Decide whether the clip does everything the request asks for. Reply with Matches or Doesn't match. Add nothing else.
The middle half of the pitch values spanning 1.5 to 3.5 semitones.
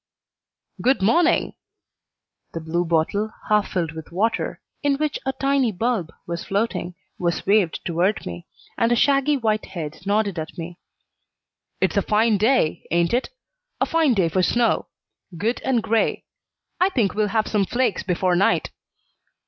Doesn't match